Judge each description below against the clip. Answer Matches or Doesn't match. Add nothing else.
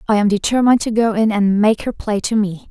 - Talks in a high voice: Matches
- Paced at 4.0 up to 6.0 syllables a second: Matches